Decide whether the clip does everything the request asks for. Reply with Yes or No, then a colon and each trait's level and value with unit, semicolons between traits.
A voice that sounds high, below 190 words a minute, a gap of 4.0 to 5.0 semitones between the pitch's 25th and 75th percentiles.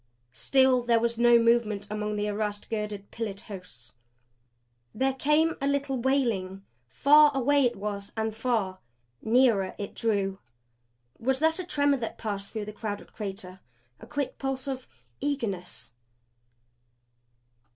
Yes: high, 225 Hz; average, 140 wpm; average, 4.7 semitones